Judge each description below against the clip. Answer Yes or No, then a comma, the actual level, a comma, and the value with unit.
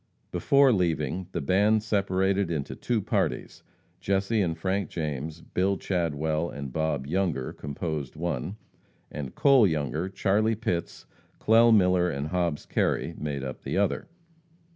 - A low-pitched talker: Yes, very low, 90 Hz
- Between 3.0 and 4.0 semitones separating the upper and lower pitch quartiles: No, average, 4.5 semitones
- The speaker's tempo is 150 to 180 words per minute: No, slow, 135 wpm